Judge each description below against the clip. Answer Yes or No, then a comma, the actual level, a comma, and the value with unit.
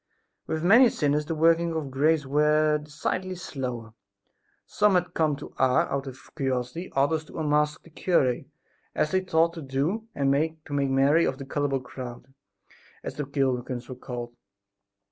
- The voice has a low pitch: No, medium, 150 Hz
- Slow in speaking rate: No, average, 165 wpm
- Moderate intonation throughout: Yes, average, 3.3 semitones